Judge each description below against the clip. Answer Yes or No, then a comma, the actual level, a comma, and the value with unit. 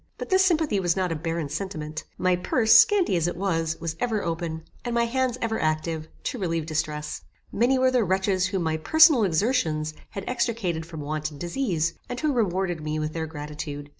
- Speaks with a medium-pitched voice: Yes, medium, 175 Hz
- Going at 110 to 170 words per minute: No, average, 195 wpm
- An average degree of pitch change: No, wide, 6.5 semitones